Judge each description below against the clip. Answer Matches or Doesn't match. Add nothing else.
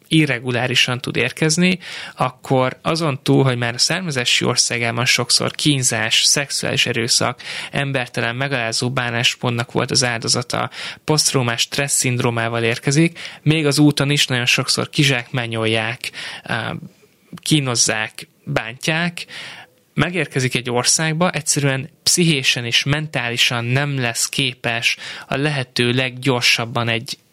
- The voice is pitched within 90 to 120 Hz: Doesn't match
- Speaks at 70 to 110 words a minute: Matches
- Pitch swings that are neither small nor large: Matches